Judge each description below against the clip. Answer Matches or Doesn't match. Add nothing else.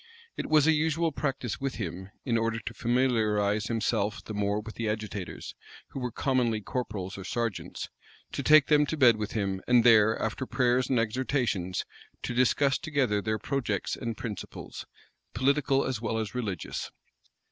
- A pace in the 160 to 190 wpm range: Matches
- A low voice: Matches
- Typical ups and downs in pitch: Matches